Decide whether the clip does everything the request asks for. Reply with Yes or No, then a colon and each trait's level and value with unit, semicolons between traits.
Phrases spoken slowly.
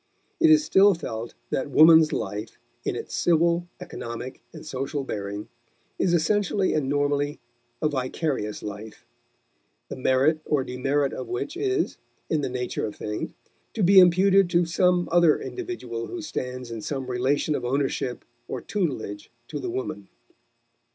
No: average, 150 wpm